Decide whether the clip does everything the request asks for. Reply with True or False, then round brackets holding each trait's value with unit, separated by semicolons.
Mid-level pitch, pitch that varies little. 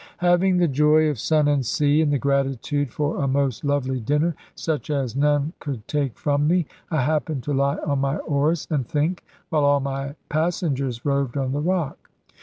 True (145 Hz; 2.1 semitones)